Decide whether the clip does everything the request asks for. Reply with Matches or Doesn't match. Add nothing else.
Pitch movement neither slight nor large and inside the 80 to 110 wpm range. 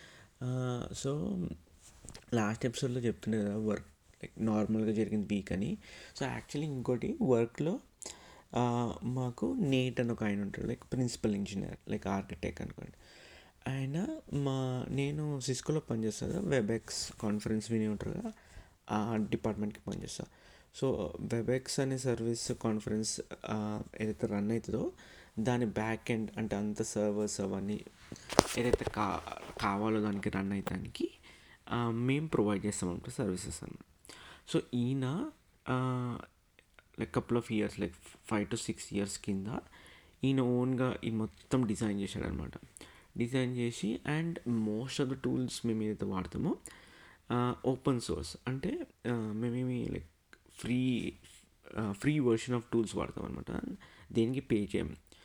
Doesn't match